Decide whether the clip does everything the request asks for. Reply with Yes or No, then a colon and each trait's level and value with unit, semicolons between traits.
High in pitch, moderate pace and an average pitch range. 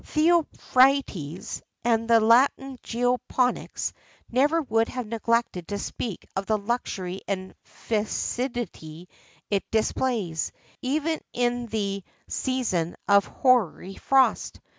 No: high, 230 Hz; slow, 100 wpm; average, 4.4 semitones